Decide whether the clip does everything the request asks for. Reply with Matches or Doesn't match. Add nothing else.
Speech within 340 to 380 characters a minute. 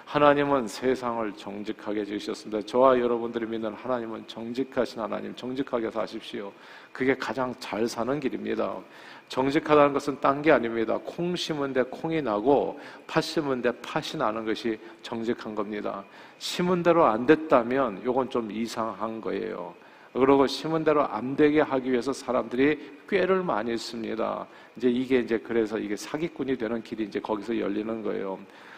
Matches